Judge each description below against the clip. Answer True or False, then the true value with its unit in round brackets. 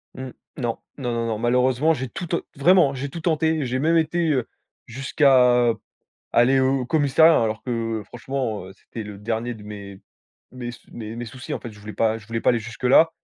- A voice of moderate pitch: False (125 Hz)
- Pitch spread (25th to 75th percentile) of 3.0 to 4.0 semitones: True (3.3 semitones)